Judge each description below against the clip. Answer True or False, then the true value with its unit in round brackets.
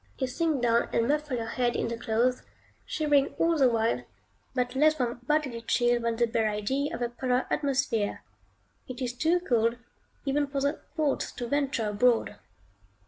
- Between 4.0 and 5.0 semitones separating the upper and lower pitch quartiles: False (3.5 semitones)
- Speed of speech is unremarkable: True (175 wpm)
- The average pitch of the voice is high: True (250 Hz)